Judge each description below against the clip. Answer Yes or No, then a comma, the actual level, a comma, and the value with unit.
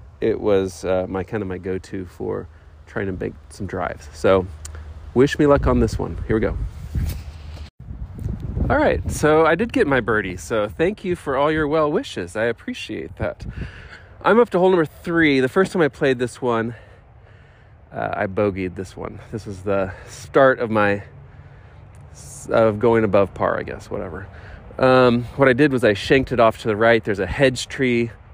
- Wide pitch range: Yes, wide, 5.7 semitones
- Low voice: Yes, low, 110 Hz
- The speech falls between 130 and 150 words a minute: No, average, 190 wpm